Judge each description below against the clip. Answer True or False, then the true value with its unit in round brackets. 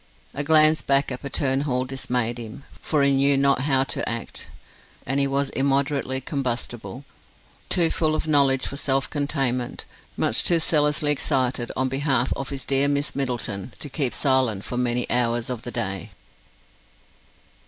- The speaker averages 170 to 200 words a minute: False (160 wpm)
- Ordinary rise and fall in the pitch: False (2.3 semitones)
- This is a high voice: False (135 Hz)